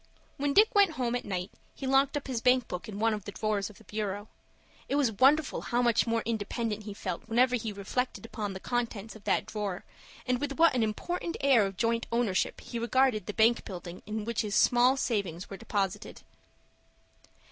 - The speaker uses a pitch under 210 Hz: No, high, 230 Hz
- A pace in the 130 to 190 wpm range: No, average, 200 wpm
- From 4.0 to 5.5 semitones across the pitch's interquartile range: No, average, 3.6 semitones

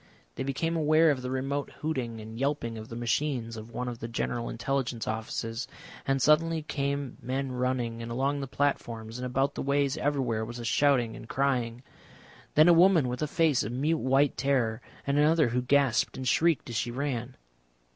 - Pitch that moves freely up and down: No, average, 3.4 semitones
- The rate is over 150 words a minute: Yes, average, 190 wpm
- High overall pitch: No, low, 130 Hz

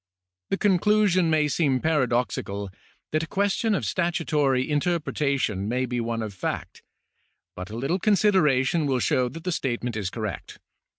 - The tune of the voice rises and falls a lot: Yes, wide, 6.2 semitones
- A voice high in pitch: No, medium, 140 Hz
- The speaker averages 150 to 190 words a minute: Yes, average, 155 wpm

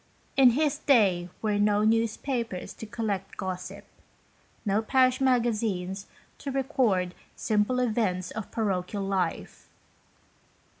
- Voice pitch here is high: Yes, high, 215 Hz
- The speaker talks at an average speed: No, slow, 110 wpm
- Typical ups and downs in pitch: Yes, average, 4.3 semitones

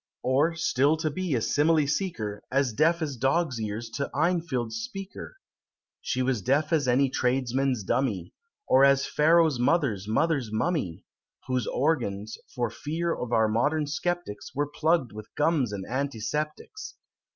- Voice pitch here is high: No, medium, 140 Hz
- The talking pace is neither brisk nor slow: Yes, average, 145 wpm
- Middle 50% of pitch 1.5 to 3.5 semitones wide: No, average, 5.2 semitones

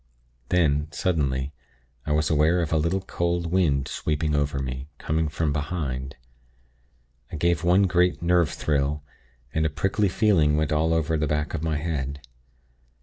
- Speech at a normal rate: Yes, average, 155 wpm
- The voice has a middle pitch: No, very low, 75 Hz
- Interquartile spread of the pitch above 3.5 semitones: No, average, 2.8 semitones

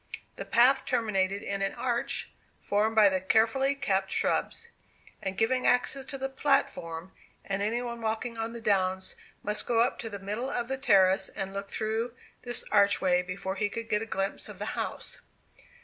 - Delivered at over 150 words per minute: Yes, average, 180 wpm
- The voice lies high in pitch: Yes, high, 220 Hz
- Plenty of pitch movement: No, average, 3.7 semitones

